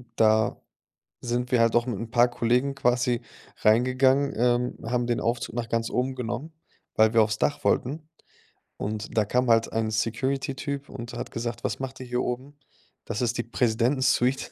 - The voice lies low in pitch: Yes, low, 120 Hz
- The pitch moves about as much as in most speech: No, narrow, 2.2 semitones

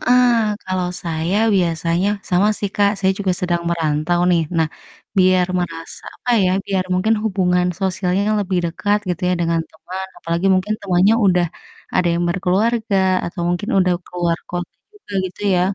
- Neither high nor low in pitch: Yes, medium, 180 Hz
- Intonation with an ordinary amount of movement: No, narrow, 2.3 semitones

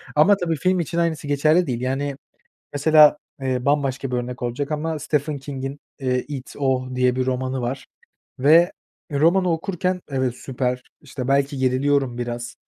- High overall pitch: No, medium, 140 Hz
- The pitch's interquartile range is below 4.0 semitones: Yes, average, 3.1 semitones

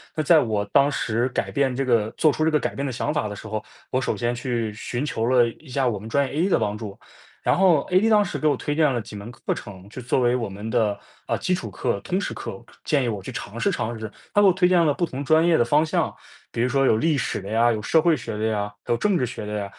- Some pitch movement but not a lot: No, wide, 5.8 semitones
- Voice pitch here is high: No, low, 125 Hz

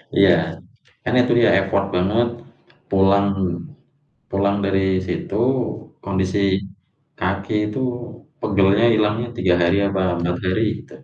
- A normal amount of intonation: No, narrow, 2.0 semitones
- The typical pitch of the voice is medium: No, low, 100 Hz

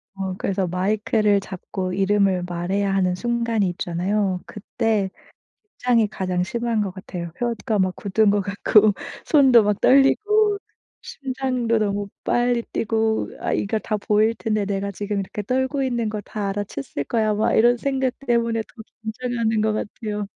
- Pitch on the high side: Yes, high, 215 Hz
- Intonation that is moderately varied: Yes, average, 3.1 semitones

